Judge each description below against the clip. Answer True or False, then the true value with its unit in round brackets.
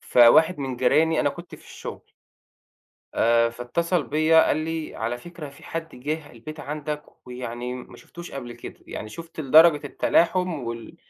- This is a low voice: False (150 Hz)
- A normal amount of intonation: True (4.8 semitones)